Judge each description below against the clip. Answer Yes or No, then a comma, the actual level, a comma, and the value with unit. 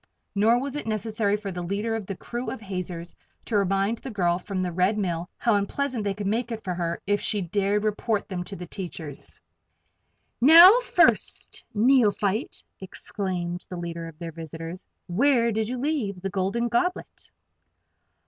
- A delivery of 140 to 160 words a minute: No, average, 170 wpm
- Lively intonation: No, average, 4.2 semitones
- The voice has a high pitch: Yes, high, 200 Hz